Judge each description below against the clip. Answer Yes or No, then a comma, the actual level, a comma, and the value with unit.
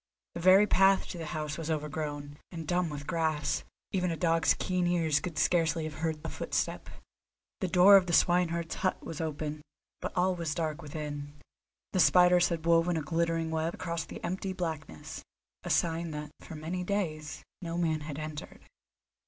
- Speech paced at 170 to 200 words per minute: Yes, average, 175 wpm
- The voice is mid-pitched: Yes, medium, 165 Hz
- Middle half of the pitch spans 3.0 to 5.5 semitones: No, narrow, 2.4 semitones